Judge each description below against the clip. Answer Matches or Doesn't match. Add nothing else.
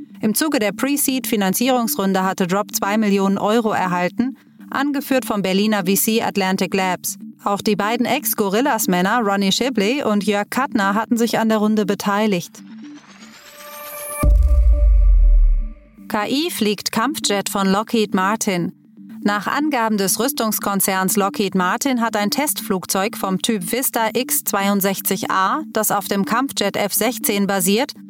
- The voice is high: Matches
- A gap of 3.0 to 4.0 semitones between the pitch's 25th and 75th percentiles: Matches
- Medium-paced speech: Doesn't match